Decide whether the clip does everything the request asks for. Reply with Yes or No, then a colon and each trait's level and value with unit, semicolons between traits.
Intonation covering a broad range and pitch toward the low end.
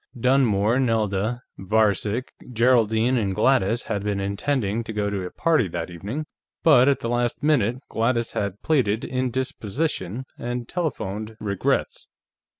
No: average, 4.0 semitones; low, 115 Hz